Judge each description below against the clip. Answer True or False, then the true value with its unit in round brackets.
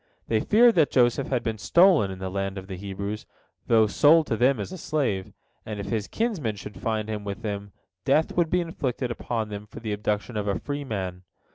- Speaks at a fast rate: True (220 wpm)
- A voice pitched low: True (110 Hz)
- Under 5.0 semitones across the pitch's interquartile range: False (5.6 semitones)